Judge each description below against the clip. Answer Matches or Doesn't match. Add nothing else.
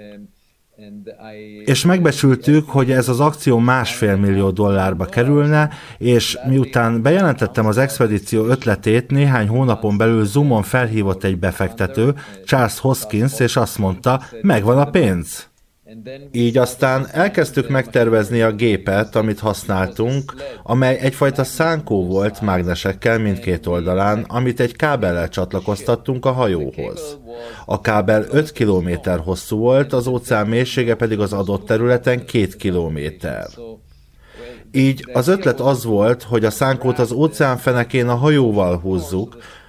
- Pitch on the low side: Matches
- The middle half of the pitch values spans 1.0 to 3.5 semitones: Doesn't match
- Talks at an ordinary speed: Matches